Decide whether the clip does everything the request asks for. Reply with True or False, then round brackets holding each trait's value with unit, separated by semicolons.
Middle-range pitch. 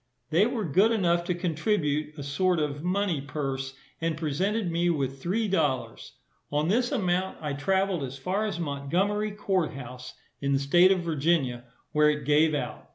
True (165 Hz)